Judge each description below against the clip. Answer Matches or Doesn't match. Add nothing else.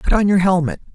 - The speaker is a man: Doesn't match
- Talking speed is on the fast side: Matches